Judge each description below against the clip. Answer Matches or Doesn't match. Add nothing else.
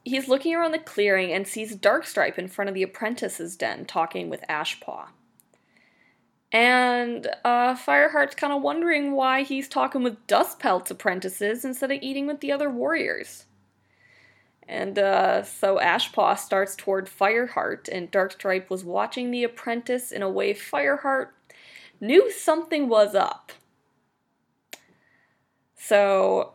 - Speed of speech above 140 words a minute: Doesn't match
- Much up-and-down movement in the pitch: Matches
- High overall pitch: Matches